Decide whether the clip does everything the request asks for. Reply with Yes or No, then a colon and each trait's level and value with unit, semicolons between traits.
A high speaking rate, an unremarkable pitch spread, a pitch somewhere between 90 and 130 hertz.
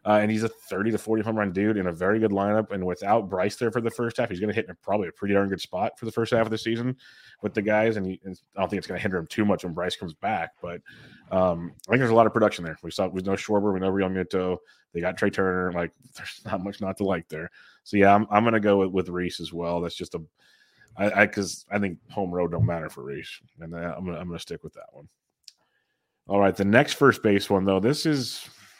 Yes: fast, 285 wpm; average, 3.1 semitones; low, 100 Hz